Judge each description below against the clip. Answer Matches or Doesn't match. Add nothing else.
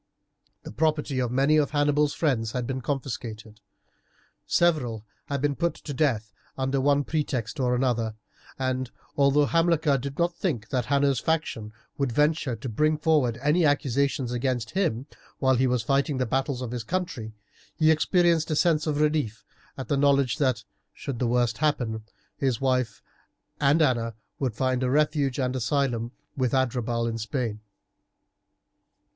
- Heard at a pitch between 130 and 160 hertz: Matches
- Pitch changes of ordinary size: Matches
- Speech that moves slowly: Doesn't match